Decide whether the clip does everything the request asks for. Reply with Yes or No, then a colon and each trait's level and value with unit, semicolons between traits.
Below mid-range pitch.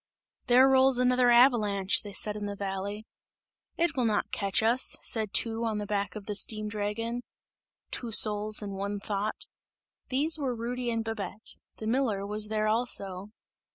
No: high, 215 Hz